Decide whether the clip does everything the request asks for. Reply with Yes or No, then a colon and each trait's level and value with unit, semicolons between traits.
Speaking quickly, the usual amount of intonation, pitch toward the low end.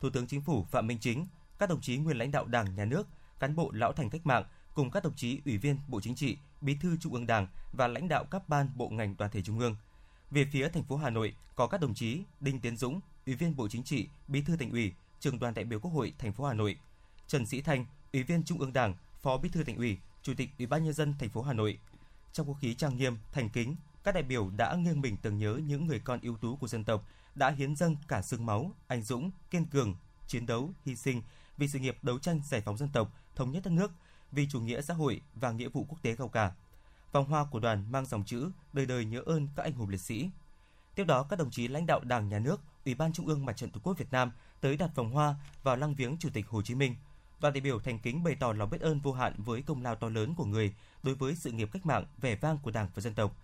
Yes: fast, 275 wpm; average, 4.6 semitones; low, 130 Hz